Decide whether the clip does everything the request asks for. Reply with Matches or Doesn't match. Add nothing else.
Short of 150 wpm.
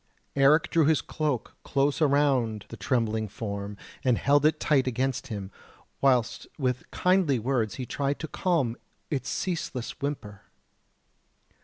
Matches